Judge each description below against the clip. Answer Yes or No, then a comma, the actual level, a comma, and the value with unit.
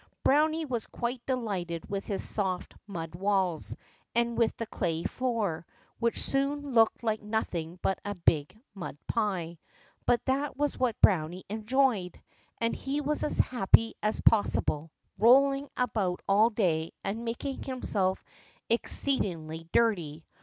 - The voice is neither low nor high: No, high, 215 Hz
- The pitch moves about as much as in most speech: No, wide, 5.7 semitones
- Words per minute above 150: No, slow, 135 wpm